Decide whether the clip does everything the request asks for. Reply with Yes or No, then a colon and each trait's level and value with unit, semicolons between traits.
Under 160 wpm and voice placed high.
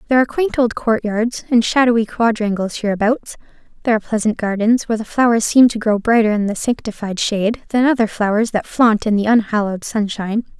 No: average, 185 wpm; high, 220 Hz